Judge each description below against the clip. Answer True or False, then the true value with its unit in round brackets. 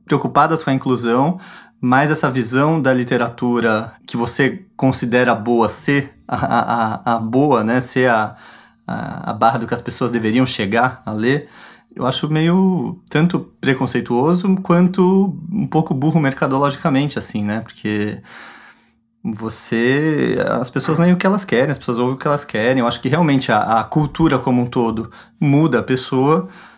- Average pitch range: True (4.7 semitones)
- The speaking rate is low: False (165 wpm)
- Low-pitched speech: True (130 Hz)